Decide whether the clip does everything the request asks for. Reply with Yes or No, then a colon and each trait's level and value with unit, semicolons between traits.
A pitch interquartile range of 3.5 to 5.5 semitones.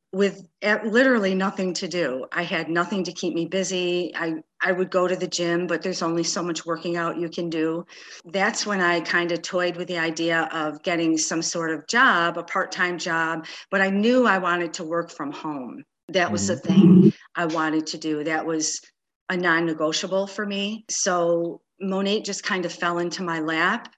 No: narrow, 2.4 semitones